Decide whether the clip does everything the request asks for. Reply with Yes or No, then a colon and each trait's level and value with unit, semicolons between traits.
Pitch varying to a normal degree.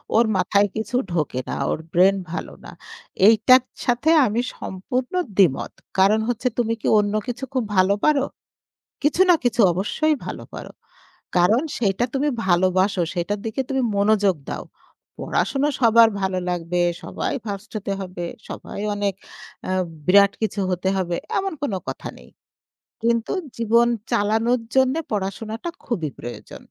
Yes: average, 4.3 semitones